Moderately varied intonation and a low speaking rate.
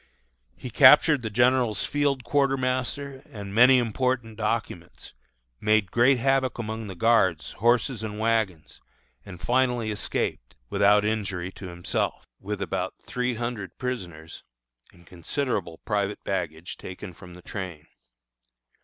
Yes: average, 4.9 semitones; slow, 125 wpm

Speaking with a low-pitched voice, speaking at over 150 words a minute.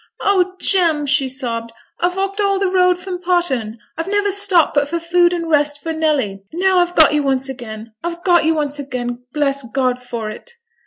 No: very high, 315 Hz; fast, 205 wpm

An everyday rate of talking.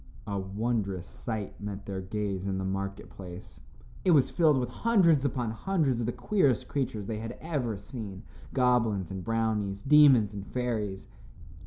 Yes: average, 160 wpm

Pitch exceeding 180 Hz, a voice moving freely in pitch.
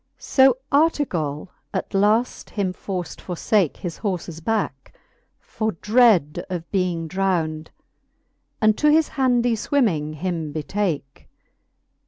Yes: high, 190 Hz; wide, 5.7 semitones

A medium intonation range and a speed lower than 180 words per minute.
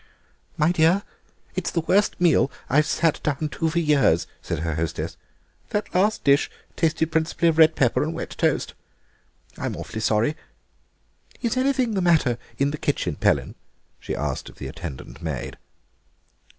Yes: average, 4.3 semitones; average, 155 wpm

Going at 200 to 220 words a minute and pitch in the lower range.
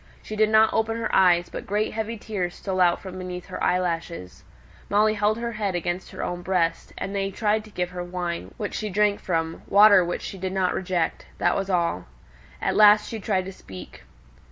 No: fast, 205 wpm; high, 190 Hz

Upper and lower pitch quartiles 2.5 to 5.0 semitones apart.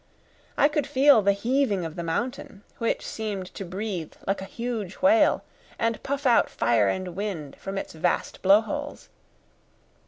No: wide, 5.6 semitones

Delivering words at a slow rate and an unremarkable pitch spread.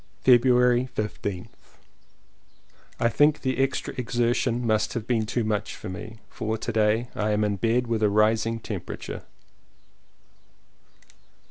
No: slow, 130 wpm; narrow, 2.3 semitones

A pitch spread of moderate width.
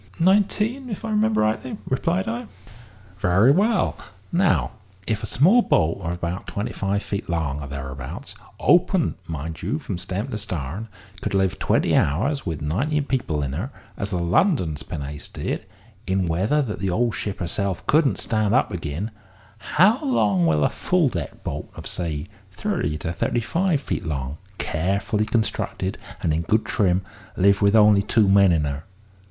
No: wide, 8.6 semitones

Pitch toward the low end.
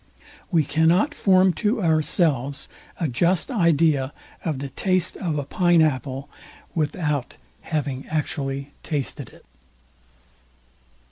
No: medium, 155 Hz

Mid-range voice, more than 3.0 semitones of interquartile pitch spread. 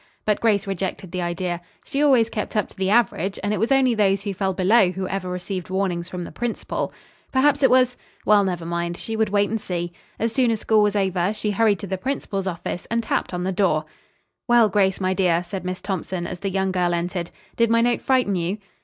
No: high, 195 Hz; average, 3.5 semitones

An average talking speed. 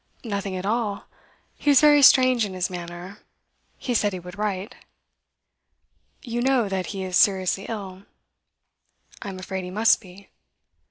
Yes: average, 155 wpm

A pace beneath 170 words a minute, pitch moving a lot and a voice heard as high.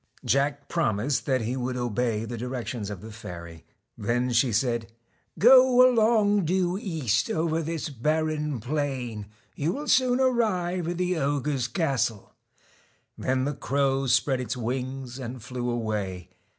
No: average, 145 wpm; wide, 5.7 semitones; low, 135 Hz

